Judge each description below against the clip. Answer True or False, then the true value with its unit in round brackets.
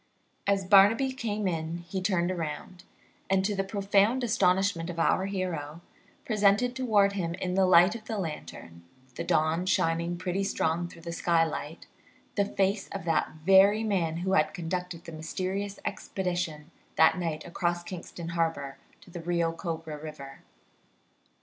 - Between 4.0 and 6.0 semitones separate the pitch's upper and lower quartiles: False (3.0 semitones)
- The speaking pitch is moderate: True (180 Hz)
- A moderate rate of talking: True (150 wpm)